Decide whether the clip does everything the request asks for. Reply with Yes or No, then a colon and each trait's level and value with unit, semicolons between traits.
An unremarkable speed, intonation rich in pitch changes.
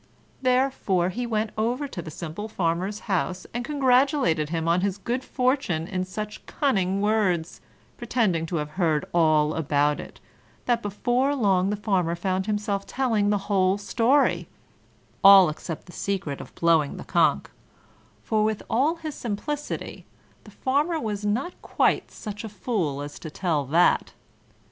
Yes: average, 155 wpm; wide, 5.8 semitones